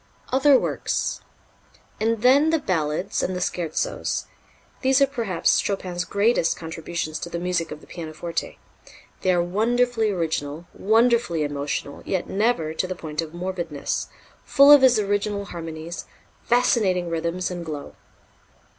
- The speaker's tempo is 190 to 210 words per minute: No, slow, 135 wpm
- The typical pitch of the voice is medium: Yes, medium, 180 Hz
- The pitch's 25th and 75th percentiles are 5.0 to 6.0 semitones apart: Yes, wide, 5.5 semitones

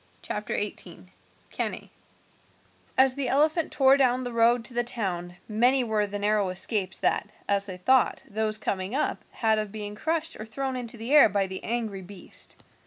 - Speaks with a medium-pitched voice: No, high, 220 Hz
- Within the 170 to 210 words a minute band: Yes, average, 175 wpm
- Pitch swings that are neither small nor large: Yes, average, 4.1 semitones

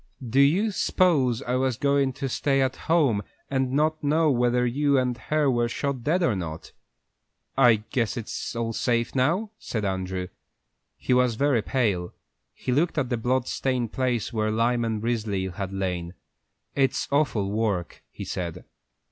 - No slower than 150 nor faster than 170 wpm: Yes, average, 160 wpm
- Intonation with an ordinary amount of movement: Yes, average, 4.3 semitones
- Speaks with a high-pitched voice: No, low, 125 Hz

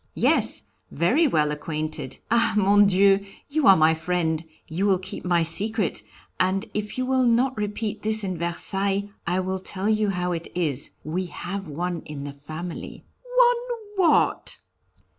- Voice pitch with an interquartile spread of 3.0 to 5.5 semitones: Yes, average, 4.4 semitones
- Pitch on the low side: No, high, 190 Hz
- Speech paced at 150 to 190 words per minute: Yes, average, 160 wpm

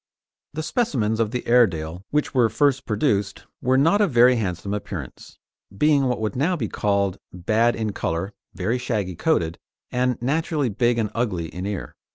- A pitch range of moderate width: Yes, average, 4.5 semitones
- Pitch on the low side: Yes, low, 115 Hz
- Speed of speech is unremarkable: Yes, average, 170 wpm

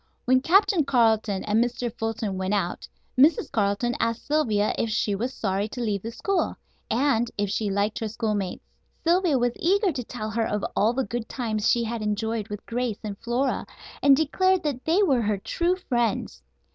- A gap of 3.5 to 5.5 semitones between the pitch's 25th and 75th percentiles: Yes, average, 4.1 semitones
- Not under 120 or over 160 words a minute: No, average, 185 wpm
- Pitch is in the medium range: No, high, 230 Hz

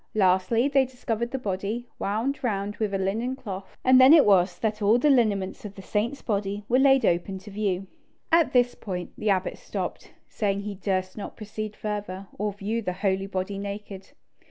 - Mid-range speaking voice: No, high, 205 Hz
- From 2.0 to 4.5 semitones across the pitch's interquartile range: Yes, average, 3.4 semitones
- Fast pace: No, average, 190 wpm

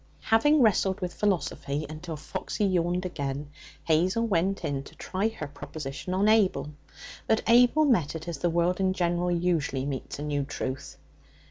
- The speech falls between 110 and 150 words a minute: No, average, 160 wpm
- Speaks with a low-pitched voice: No, medium, 175 Hz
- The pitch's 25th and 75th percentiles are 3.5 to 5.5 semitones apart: Yes, average, 4.8 semitones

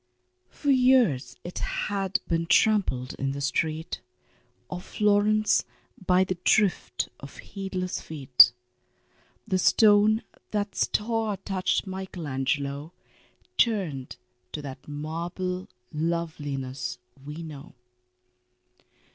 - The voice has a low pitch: No, medium, 175 Hz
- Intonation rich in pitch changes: Yes, wide, 5.8 semitones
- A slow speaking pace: Yes, slow, 95 wpm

